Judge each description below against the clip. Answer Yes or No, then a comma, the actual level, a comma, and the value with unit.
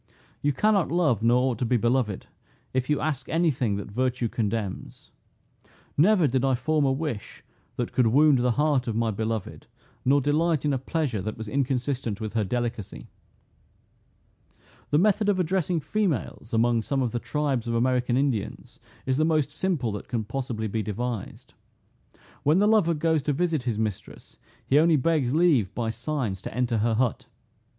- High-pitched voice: No, low, 130 Hz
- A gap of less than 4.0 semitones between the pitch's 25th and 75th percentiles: No, average, 4.9 semitones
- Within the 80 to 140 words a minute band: No, average, 175 wpm